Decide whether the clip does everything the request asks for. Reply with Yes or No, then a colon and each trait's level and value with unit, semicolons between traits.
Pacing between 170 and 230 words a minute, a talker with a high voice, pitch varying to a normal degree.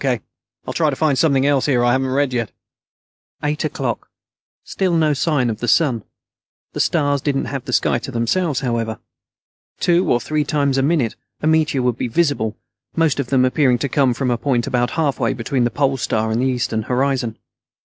No: average, 195 wpm; low, 135 Hz; average, 3.3 semitones